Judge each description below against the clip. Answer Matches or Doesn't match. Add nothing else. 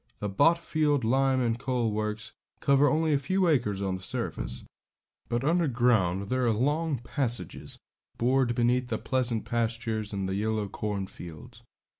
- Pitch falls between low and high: Doesn't match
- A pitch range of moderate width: Matches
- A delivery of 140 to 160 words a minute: Matches